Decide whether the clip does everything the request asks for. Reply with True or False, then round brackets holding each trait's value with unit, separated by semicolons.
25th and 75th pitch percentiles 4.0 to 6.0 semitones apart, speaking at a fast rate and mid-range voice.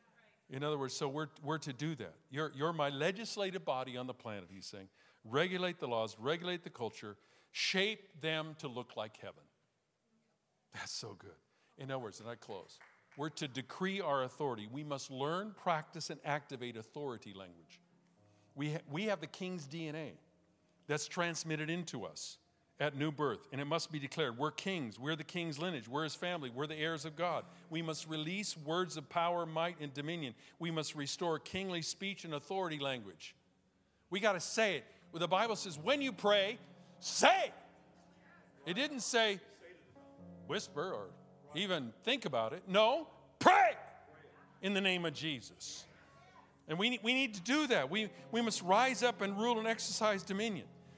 False (5.1 semitones; 175 wpm; 165 Hz)